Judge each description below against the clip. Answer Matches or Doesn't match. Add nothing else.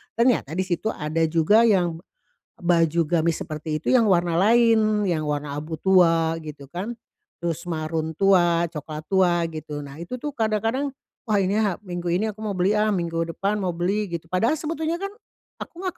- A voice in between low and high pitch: Matches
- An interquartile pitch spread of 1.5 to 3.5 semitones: Doesn't match